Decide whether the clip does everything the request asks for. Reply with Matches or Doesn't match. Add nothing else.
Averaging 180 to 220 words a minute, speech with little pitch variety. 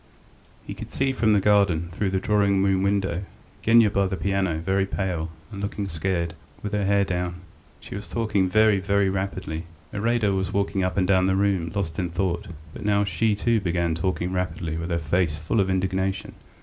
Matches